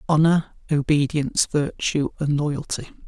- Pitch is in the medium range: Yes, medium, 150 Hz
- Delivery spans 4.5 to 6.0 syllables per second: No, 4.3 syllables/s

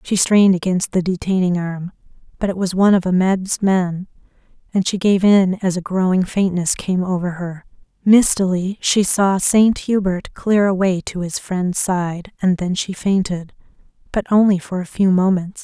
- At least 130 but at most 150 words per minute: No, average, 175 wpm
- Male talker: No, female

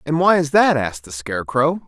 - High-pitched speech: No, medium, 145 Hz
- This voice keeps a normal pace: No, fast, 225 wpm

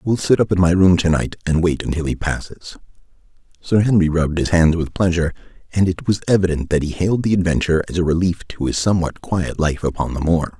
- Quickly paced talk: Yes, fast, 220 wpm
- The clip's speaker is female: No, male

